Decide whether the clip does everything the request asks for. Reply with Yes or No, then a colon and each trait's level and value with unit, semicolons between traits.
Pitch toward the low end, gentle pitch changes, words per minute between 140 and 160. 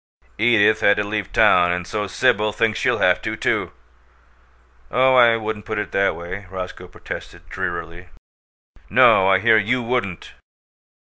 No: low, 105 Hz; average, 3.2 semitones; average, 150 wpm